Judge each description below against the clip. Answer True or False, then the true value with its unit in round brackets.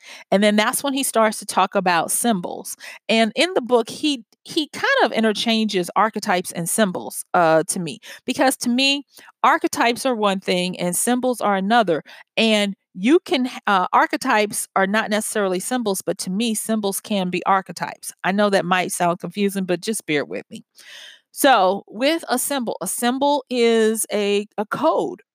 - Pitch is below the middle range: False (215 Hz)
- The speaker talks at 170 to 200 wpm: True (175 wpm)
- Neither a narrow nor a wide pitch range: True (4.4 semitones)